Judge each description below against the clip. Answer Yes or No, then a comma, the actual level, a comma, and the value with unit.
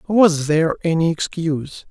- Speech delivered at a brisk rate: No, slow, 125 wpm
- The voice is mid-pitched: Yes, medium, 165 Hz